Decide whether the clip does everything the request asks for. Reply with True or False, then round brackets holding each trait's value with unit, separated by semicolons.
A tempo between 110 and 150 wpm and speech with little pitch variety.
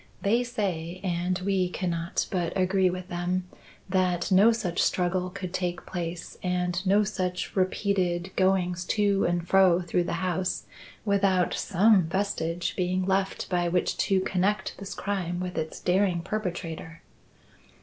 True (140 wpm; 1.6 semitones)